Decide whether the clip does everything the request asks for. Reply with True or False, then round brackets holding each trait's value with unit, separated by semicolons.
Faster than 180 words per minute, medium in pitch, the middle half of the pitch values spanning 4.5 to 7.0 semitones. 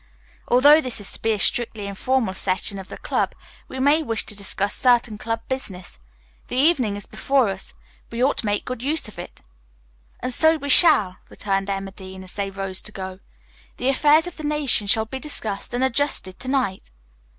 False (195 wpm; 225 Hz; 5.3 semitones)